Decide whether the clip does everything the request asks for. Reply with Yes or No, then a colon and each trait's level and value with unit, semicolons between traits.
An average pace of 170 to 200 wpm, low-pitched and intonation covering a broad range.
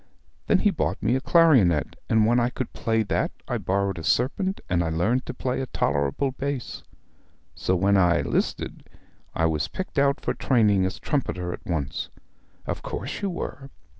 Yes: average, 180 wpm; low, 110 Hz; wide, 7.4 semitones